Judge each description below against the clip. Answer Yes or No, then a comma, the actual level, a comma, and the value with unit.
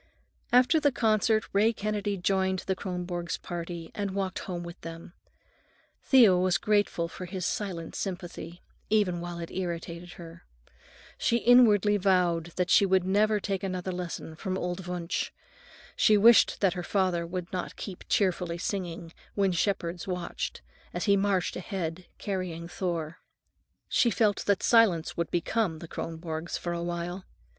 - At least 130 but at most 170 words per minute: Yes, average, 150 wpm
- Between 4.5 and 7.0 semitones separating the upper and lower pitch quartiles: No, average, 2.7 semitones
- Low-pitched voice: No, medium, 185 Hz